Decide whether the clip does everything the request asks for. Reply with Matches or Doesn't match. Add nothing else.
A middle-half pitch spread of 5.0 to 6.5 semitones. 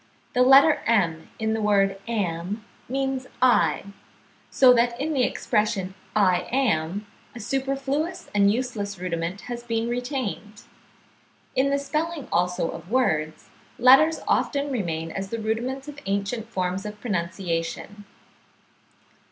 Matches